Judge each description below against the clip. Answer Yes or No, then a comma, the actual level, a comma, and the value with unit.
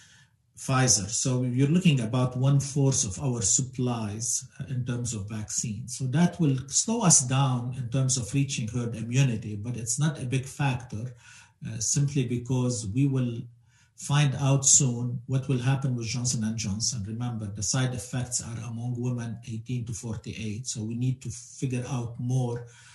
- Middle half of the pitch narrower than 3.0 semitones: Yes, narrow, 2.4 semitones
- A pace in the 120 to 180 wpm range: Yes, average, 170 wpm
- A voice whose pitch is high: No, low, 125 Hz